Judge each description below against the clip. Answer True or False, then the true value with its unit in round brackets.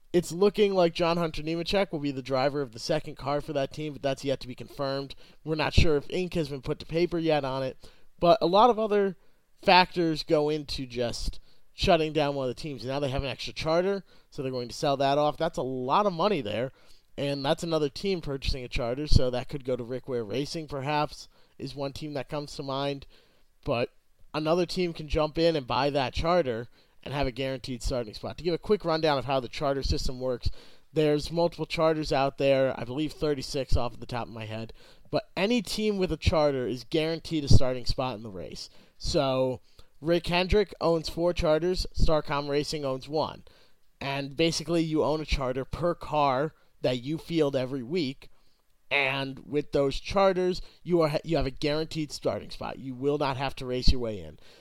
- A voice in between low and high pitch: True (145 Hz)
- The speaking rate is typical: False (210 wpm)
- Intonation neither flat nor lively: True (3.7 semitones)